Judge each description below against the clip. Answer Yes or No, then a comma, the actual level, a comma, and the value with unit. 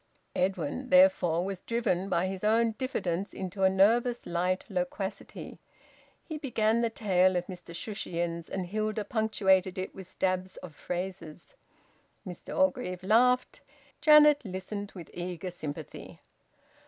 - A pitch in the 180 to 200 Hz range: Yes, high, 190 Hz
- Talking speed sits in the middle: No, slow, 130 wpm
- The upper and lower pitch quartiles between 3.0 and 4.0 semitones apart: Yes, average, 3.7 semitones